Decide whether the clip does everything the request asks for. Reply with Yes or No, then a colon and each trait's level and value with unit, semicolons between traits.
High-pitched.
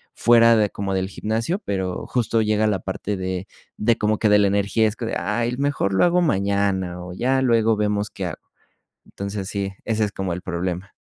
No: low, 105 Hz